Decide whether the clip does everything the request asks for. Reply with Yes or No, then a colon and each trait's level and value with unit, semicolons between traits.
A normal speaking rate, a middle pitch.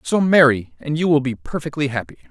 No: fast, 210 wpm; medium, 145 Hz